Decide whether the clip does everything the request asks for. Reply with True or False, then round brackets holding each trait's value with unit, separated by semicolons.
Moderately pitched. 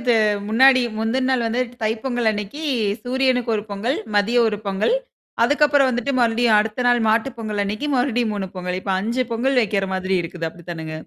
False (225 Hz)